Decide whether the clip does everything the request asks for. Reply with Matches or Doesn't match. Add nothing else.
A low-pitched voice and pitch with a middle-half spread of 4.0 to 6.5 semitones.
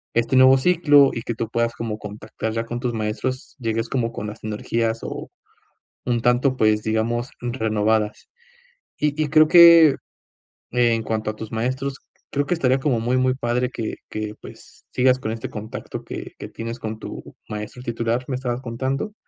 Doesn't match